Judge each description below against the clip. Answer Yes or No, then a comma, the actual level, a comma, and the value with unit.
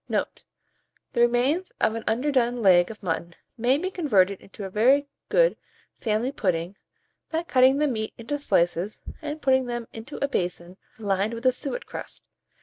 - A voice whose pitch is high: Yes, high, 235 Hz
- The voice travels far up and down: Yes, wide, 5.8 semitones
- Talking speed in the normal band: Yes, average, 165 wpm